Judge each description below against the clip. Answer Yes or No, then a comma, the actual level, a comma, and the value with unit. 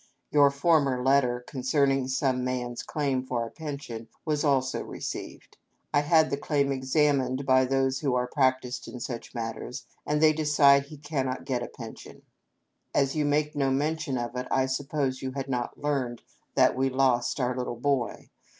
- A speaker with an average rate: Yes, average, 180 wpm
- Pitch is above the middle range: No, low, 135 Hz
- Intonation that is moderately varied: No, narrow, 2.2 semitones